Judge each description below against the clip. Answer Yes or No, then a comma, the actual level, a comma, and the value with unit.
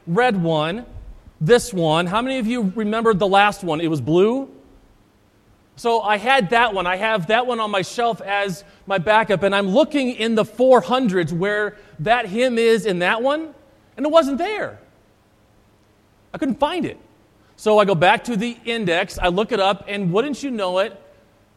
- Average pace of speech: Yes, average, 185 wpm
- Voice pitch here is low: No, high, 210 Hz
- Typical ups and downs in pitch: No, wide, 5.7 semitones